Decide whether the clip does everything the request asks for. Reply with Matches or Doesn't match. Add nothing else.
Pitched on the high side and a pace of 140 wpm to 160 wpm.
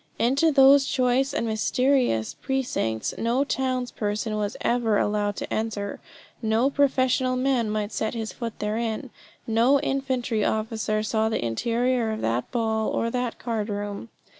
Matches